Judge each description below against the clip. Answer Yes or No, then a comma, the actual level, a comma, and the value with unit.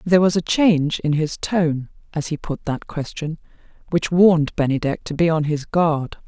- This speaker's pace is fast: No, average, 190 wpm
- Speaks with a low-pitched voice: No, medium, 160 Hz